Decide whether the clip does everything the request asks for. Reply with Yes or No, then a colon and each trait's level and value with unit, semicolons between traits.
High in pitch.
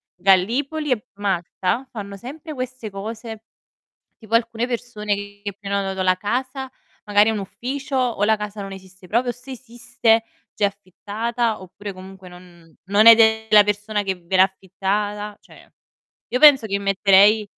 Yes: high, 210 Hz